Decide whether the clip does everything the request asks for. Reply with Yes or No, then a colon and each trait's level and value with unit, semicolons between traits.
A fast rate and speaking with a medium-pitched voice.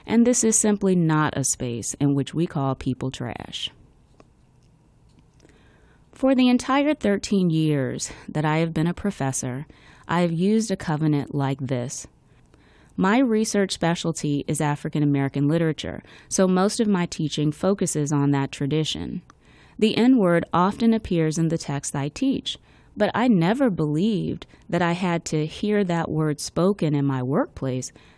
No: average, 155 wpm; medium, 165 Hz